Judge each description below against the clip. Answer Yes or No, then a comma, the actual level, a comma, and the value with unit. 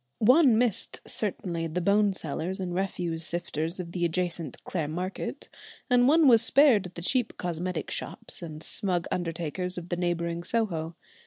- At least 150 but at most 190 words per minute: Yes, average, 155 wpm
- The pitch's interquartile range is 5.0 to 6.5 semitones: No, average, 3.5 semitones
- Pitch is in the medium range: Yes, medium, 180 Hz